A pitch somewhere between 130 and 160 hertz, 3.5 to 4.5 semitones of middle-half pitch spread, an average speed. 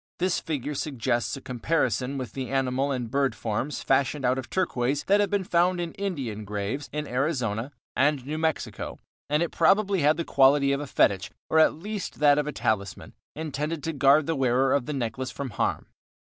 Yes: medium, 140 Hz; average, 3.8 semitones; average, 190 wpm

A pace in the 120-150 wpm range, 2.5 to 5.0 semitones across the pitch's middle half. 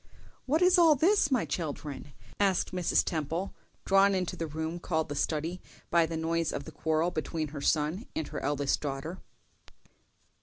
No: average, 165 wpm; average, 3.8 semitones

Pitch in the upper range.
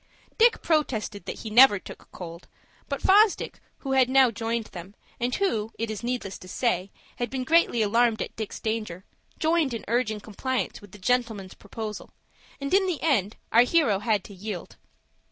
Yes: high, 230 Hz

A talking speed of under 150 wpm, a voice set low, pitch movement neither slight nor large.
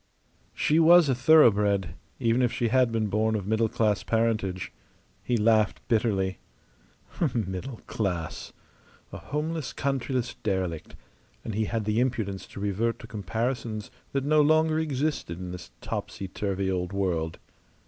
Yes: average, 140 wpm; low, 110 Hz; average, 4.6 semitones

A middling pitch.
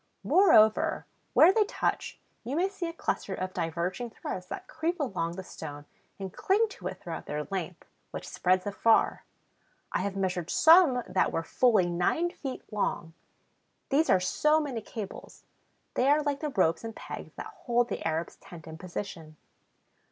No: high, 210 Hz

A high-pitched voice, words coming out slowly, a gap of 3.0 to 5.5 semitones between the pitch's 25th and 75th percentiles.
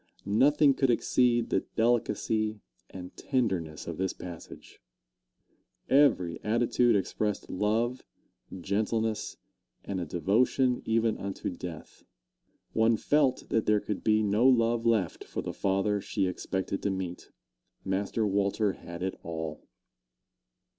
No: low, 105 Hz; slow, 120 wpm; average, 3.6 semitones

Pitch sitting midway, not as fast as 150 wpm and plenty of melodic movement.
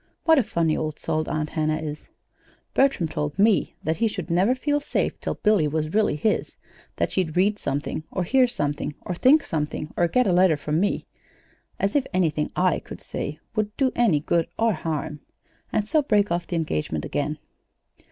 No: medium, 175 Hz; average, 185 wpm; wide, 5.7 semitones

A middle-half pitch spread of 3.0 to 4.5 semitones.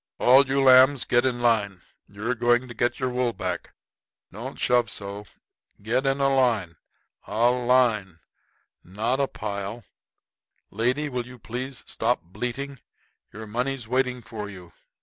Yes: average, 3.3 semitones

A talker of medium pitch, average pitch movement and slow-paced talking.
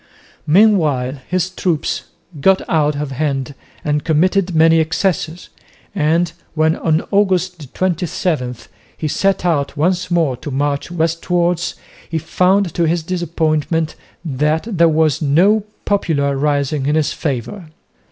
Yes: medium, 160 Hz; average, 3.2 semitones; slow, 125 wpm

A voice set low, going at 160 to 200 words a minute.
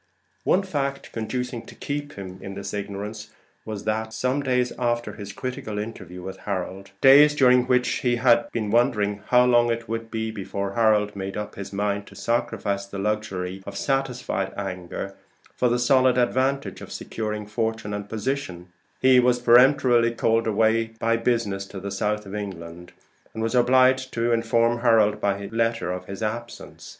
Yes: low, 110 Hz; average, 170 wpm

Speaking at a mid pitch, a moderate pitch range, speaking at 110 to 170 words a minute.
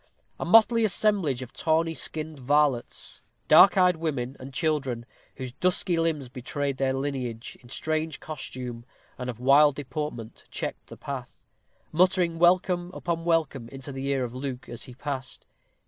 Yes: medium, 145 Hz; average, 4.3 semitones; average, 150 wpm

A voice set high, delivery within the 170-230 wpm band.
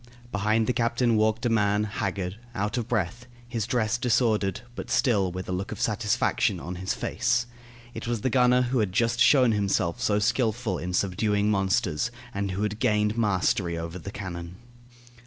No: low, 105 Hz; average, 180 wpm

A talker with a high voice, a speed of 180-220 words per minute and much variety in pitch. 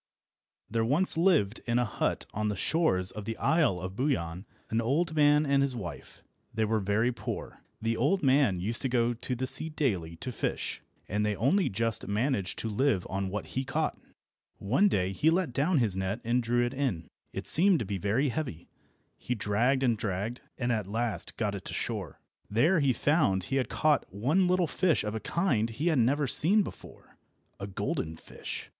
No: low, 120 Hz; average, 200 wpm; wide, 6.0 semitones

